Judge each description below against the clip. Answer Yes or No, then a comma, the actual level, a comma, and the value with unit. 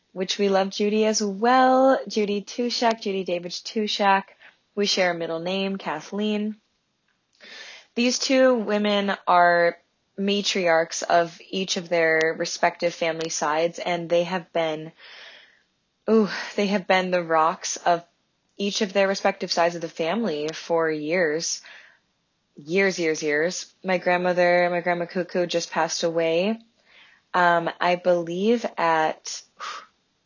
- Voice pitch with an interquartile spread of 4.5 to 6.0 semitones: No, average, 3.3 semitones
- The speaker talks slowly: Yes, slow, 130 wpm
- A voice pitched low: No, medium, 180 Hz